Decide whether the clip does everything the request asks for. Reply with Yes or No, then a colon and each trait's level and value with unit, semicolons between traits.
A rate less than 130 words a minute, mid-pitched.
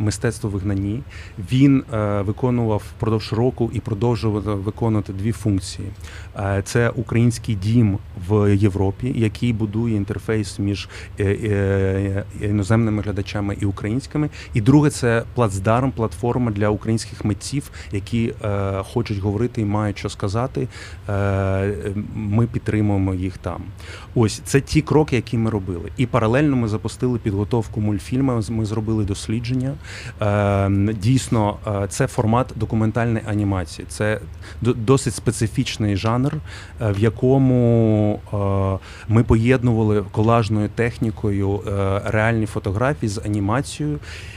No: average, 115 wpm; low, 110 Hz